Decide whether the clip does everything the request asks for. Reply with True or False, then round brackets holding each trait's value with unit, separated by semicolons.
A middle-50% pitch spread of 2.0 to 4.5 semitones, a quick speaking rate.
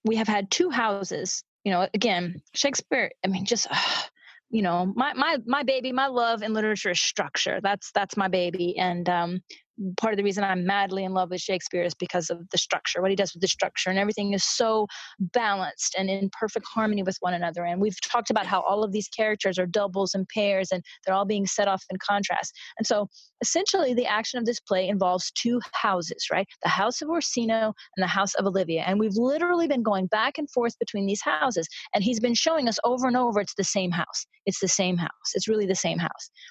True (3.9 semitones; 225 wpm)